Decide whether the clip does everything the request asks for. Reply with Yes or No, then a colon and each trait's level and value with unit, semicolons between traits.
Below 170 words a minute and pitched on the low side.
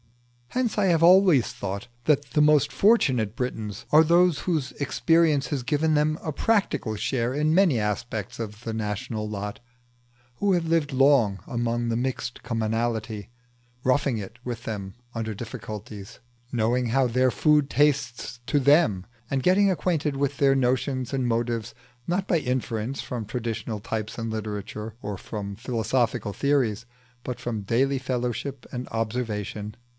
Yes: average, 150 wpm; low, 125 Hz